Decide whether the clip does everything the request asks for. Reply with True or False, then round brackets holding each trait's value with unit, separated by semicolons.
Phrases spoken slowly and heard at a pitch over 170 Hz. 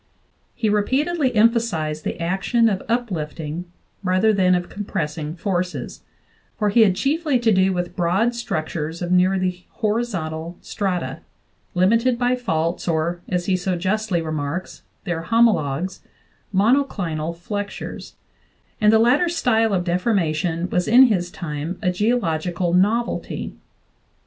True (130 wpm; 185 Hz)